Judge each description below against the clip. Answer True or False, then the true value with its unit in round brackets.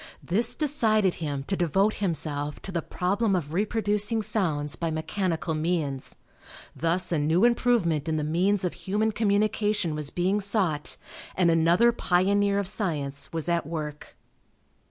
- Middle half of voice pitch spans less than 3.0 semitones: False (4.5 semitones)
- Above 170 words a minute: False (145 wpm)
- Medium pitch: True (180 Hz)